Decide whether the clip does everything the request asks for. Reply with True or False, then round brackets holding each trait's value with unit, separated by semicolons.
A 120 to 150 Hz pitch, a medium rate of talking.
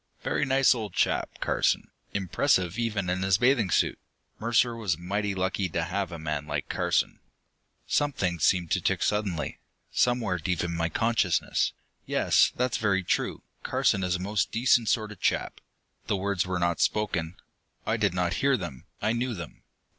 False (95 Hz; 170 wpm)